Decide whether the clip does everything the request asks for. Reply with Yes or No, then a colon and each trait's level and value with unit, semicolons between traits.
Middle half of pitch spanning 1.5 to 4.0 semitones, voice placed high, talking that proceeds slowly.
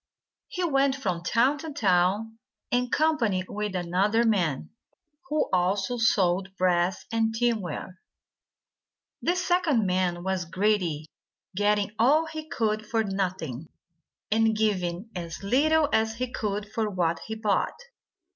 No: average, 4.4 semitones; high, 210 Hz; slow, 125 wpm